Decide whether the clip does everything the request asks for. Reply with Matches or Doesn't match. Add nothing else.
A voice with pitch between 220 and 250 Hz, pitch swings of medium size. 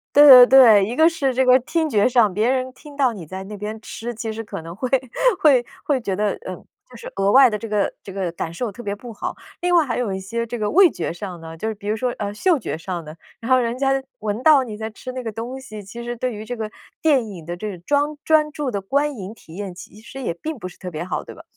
Matches